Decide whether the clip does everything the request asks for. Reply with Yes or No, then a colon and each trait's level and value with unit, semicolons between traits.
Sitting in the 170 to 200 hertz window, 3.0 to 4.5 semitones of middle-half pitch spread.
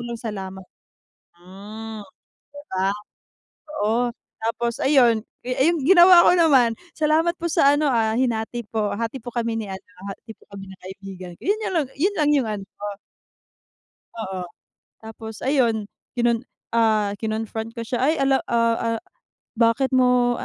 No: high, 230 Hz; average, 3.4 semitones